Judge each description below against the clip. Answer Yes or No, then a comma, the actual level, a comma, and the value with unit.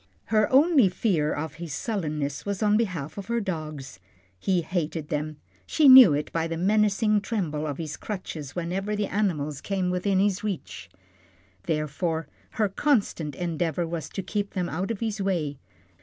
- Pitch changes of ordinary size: Yes, average, 5.0 semitones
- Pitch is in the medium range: Yes, medium, 180 Hz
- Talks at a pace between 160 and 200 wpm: Yes, average, 165 wpm